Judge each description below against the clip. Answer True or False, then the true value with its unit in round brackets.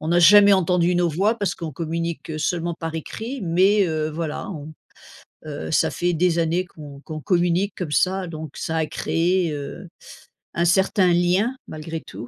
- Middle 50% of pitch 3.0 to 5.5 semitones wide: False (2.6 semitones)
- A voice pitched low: False (170 Hz)